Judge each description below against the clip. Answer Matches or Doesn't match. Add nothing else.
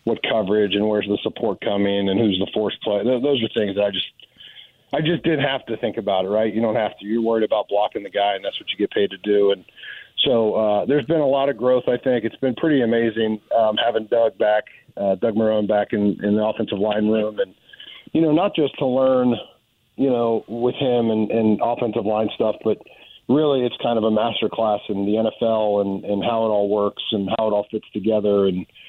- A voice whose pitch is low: Matches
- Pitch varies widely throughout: Doesn't match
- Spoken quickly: Matches